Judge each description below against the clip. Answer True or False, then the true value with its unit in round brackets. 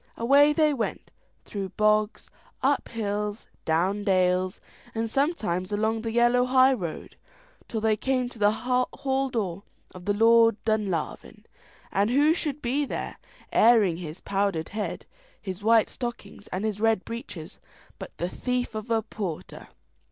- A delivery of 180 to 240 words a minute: False (150 wpm)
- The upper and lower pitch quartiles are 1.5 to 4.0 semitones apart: True (3.7 semitones)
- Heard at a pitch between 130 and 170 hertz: False (220 Hz)